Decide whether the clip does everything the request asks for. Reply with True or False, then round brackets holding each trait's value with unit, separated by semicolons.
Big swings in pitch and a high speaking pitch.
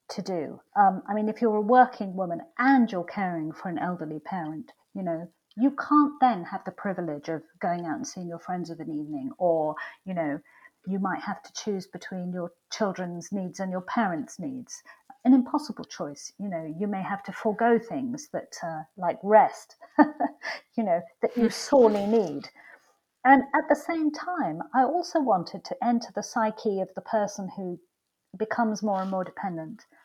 True (6.0 semitones; 205 Hz)